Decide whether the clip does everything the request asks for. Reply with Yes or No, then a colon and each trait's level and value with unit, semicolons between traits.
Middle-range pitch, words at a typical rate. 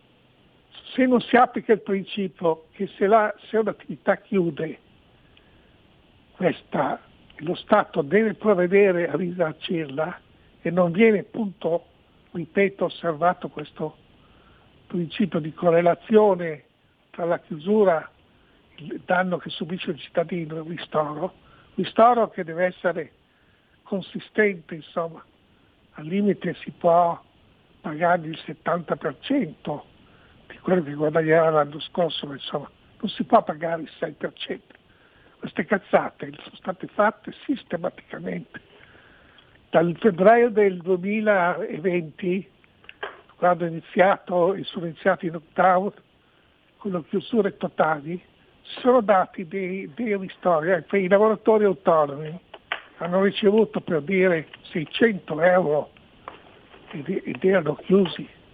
No: medium, 180 Hz; slow, 110 wpm